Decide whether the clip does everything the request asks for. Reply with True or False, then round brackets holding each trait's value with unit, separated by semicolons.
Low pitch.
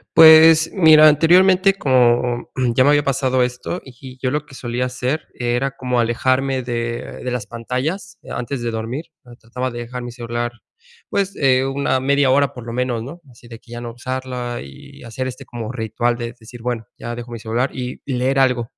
True (125 Hz)